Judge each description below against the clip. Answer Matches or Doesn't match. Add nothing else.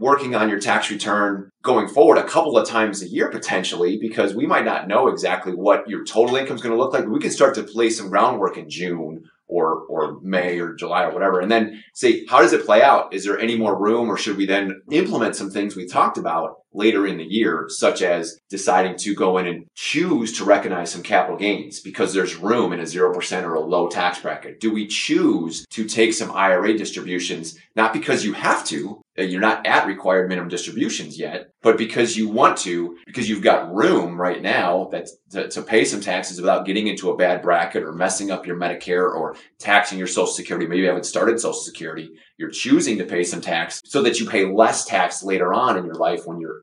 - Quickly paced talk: Matches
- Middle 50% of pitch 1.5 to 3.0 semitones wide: Doesn't match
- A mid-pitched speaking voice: Doesn't match